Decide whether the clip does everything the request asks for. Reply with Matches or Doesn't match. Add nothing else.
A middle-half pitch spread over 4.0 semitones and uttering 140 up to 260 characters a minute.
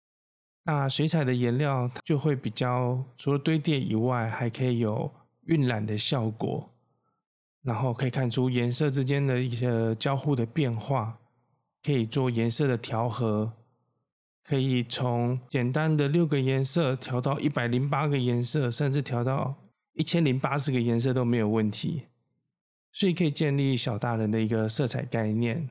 Doesn't match